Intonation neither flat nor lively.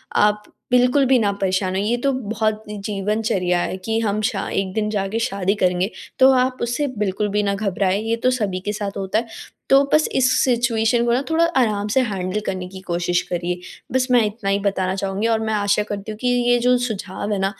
Yes: average, 3.5 semitones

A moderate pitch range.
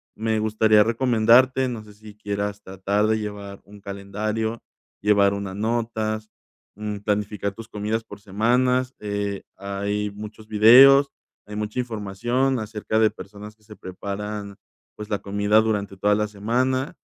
No: narrow, 1.6 semitones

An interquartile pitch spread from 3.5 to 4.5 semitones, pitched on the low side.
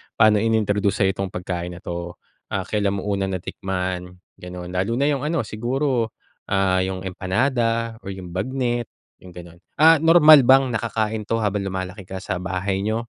Yes: average, 3.8 semitones; low, 100 Hz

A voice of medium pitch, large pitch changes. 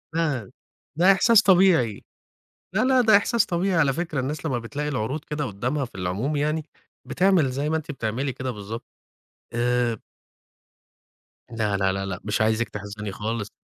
No: low, 130 Hz; wide, 6.7 semitones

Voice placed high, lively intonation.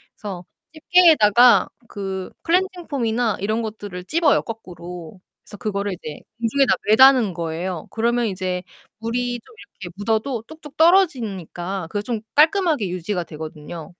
Yes: high, 215 Hz; wide, 6.1 semitones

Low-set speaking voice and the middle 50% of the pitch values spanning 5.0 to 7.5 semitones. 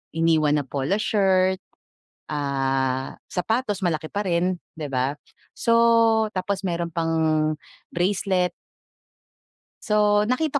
No: medium, 185 Hz; average, 5.3 semitones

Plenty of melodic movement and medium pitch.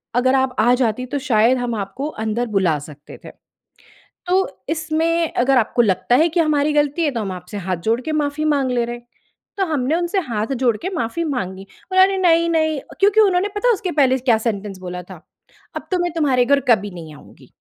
No: wide, 6.7 semitones; very high, 260 Hz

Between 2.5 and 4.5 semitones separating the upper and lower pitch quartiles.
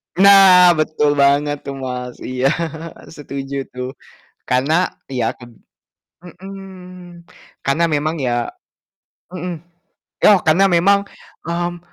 No: average, 4.9 semitones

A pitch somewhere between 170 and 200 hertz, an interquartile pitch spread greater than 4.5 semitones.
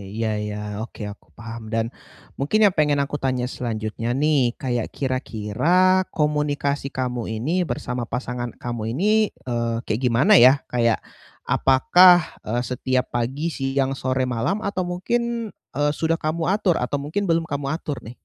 No: low, 135 Hz; average, 5.1 semitones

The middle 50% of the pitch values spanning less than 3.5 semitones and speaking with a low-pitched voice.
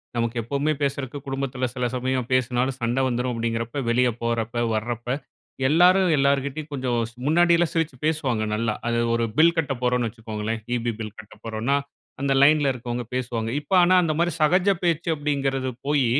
No: average, 4.0 semitones; low, 130 Hz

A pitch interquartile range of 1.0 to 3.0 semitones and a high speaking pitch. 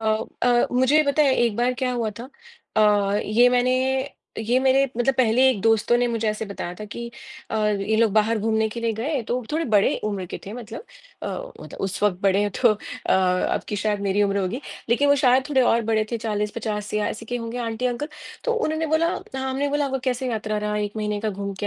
No: average, 3.4 semitones; high, 225 Hz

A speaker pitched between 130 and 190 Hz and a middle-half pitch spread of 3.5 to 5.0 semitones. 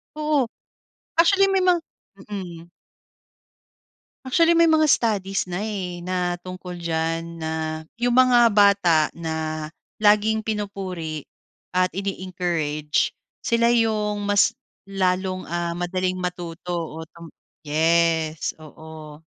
Yes: medium, 185 Hz; average, 4.2 semitones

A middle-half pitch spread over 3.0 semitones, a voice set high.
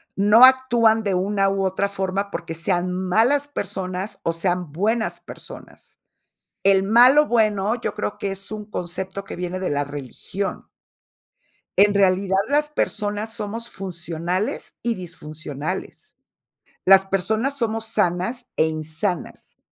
Yes: average, 3.4 semitones; high, 195 Hz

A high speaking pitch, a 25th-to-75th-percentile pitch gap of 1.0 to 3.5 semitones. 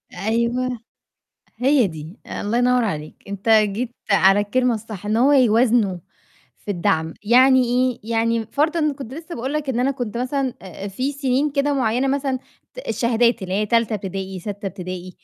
No: high, 235 Hz; average, 4.3 semitones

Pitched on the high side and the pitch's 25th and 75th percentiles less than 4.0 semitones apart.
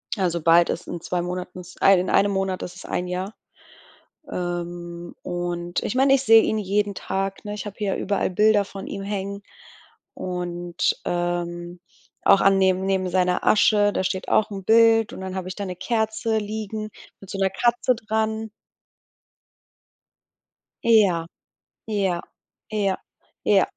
Yes: high, 195 Hz; average, 2.9 semitones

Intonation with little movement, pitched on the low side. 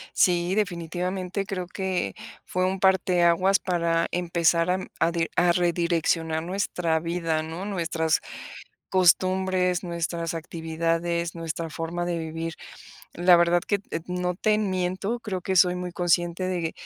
No: narrow, 1.7 semitones; medium, 175 Hz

